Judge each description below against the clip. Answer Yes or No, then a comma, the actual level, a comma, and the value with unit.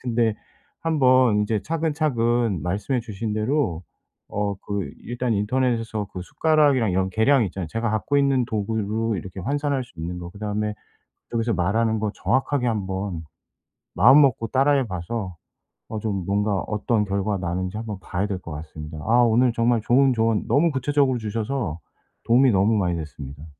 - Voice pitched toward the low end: Yes, low, 110 Hz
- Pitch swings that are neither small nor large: Yes, average, 4.4 semitones